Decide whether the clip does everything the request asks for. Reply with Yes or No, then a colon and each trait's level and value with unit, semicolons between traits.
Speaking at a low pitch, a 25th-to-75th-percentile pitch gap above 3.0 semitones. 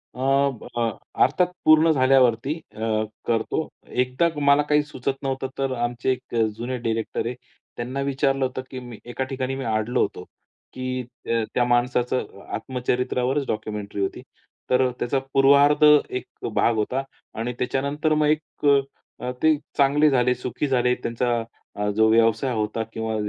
No: low, 125 Hz; narrow, 2.5 semitones